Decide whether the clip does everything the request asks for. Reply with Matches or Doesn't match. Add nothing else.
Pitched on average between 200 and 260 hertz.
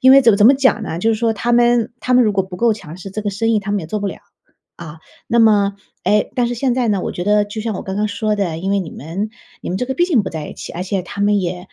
Matches